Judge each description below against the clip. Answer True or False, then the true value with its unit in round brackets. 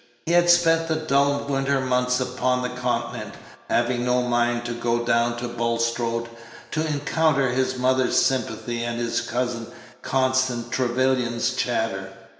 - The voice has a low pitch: True (125 Hz)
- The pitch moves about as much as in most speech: False (1.9 semitones)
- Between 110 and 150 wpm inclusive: True (140 wpm)